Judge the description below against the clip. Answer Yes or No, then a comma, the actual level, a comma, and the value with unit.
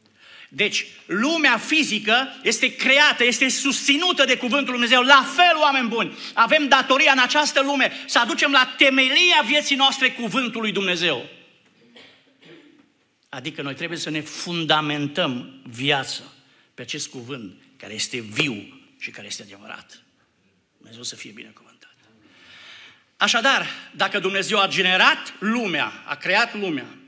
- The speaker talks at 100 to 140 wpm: Yes, average, 130 wpm